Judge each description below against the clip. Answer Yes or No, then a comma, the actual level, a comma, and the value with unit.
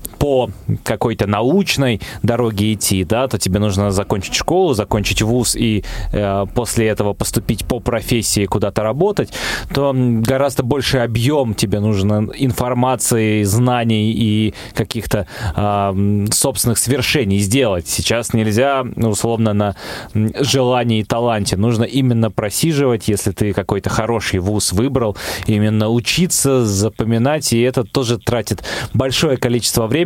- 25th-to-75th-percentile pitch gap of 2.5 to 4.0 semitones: Yes, average, 3.3 semitones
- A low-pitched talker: Yes, low, 115 Hz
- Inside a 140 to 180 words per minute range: No, average, 125 wpm